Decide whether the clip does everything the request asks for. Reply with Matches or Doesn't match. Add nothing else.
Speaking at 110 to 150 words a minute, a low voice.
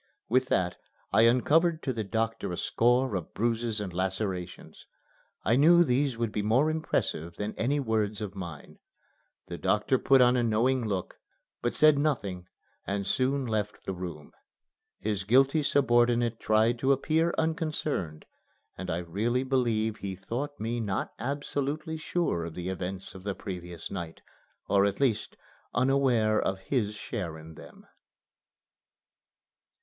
Matches